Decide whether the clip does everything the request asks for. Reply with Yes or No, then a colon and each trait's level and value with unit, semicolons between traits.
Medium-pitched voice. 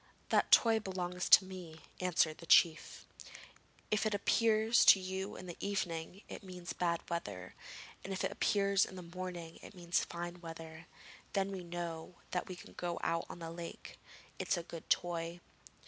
Yes: medium, 175 Hz